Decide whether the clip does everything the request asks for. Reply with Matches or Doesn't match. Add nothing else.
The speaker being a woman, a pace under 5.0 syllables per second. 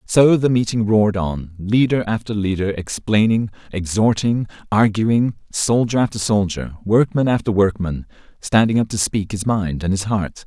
Doesn't match